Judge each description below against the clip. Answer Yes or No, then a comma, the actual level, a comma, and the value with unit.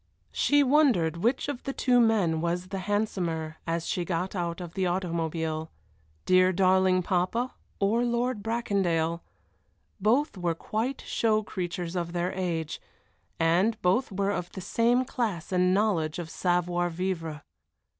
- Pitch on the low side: No, medium, 185 Hz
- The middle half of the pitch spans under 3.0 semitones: No, average, 4.2 semitones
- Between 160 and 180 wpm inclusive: No, average, 145 wpm